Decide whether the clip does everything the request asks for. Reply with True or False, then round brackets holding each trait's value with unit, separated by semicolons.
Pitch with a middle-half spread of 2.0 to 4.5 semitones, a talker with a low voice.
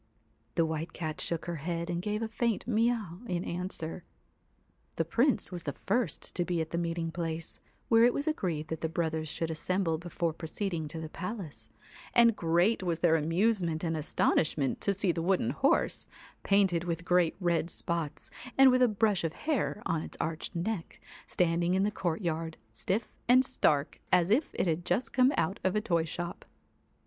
False (3.8 semitones; 175 Hz)